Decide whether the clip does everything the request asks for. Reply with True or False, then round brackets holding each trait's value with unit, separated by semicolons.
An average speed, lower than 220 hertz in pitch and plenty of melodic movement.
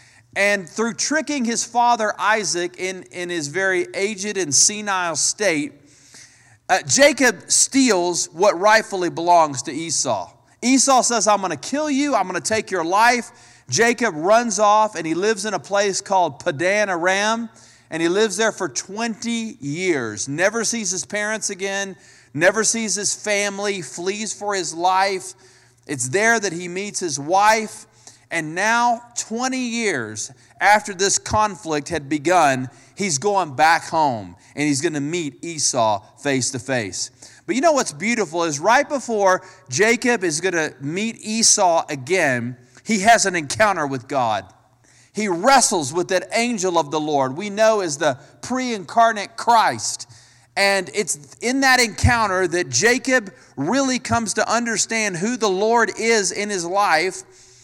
True (155 wpm; 190 Hz; 6.4 semitones)